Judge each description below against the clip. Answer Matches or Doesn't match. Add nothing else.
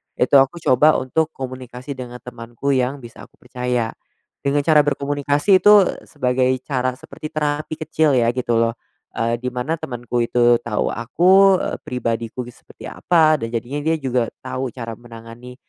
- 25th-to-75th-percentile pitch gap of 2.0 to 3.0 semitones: Doesn't match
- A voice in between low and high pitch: Doesn't match